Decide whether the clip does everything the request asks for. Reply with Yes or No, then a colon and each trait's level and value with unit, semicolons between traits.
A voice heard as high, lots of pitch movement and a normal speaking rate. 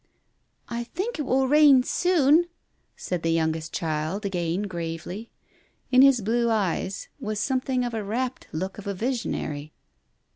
Yes: high, 215 Hz; wide, 7.0 semitones; average, 155 wpm